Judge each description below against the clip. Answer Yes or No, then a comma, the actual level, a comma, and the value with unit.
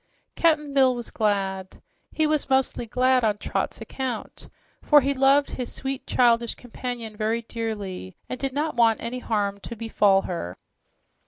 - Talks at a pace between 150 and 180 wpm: Yes, average, 155 wpm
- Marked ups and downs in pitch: No, average, 3.8 semitones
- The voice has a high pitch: Yes, high, 235 Hz